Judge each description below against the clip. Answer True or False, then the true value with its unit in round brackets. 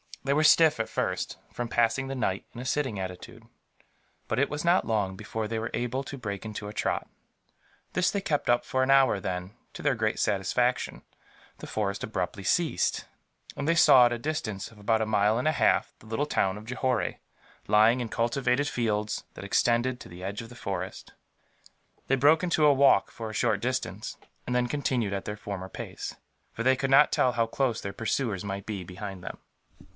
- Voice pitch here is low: True (115 Hz)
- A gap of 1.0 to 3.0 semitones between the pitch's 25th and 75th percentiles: False (4.3 semitones)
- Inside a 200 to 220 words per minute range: True (205 wpm)